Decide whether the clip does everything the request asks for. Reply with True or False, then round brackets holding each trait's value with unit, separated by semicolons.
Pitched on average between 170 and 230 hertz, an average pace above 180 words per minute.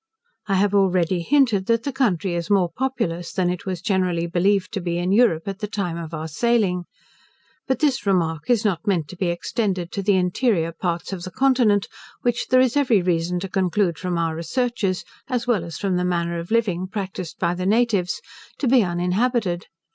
True (190 Hz; 200 wpm)